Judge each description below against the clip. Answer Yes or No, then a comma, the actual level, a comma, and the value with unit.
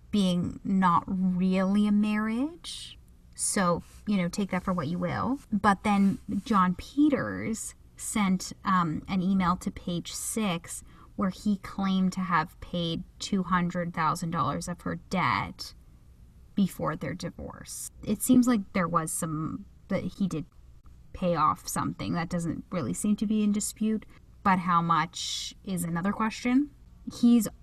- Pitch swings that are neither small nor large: Yes, average, 3.4 semitones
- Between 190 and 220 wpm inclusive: No, average, 150 wpm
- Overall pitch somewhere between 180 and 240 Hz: Yes, high, 190 Hz